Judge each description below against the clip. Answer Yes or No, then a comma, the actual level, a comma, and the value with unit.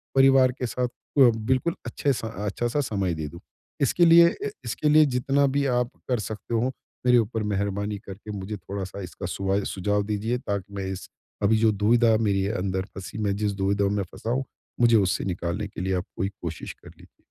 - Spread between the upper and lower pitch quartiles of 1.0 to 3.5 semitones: No, average, 4.1 semitones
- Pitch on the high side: No, low, 105 Hz